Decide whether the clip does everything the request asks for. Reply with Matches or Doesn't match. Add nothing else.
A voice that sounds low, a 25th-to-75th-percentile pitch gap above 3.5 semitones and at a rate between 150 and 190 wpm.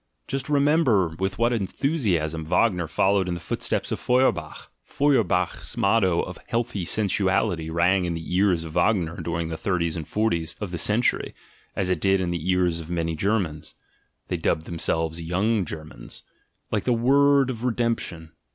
Matches